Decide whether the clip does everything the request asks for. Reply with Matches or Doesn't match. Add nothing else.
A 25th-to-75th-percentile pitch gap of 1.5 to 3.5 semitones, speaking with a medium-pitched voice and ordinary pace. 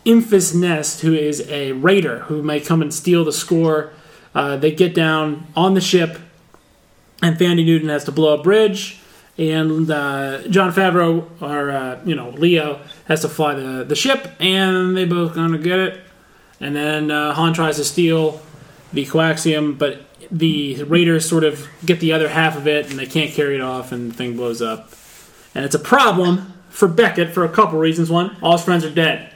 Matches